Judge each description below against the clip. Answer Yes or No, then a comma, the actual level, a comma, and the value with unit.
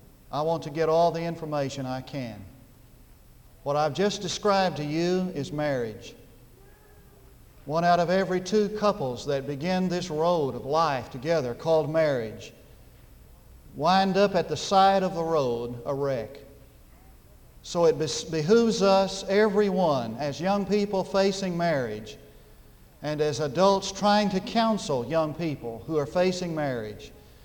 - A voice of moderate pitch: Yes, medium, 165 Hz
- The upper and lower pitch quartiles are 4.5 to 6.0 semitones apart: Yes, average, 5.2 semitones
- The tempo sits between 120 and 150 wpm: Yes, average, 140 wpm